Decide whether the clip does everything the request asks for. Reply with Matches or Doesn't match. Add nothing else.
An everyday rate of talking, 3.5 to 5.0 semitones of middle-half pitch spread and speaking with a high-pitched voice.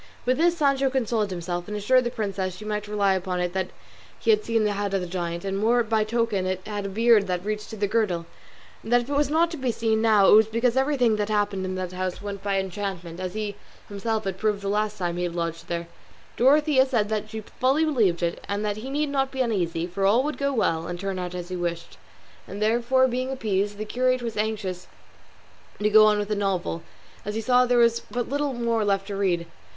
Doesn't match